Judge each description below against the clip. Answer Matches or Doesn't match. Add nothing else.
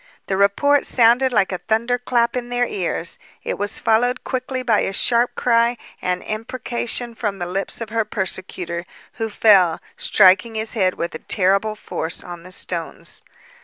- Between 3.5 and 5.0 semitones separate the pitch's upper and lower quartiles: Matches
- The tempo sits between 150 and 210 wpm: Matches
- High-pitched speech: Matches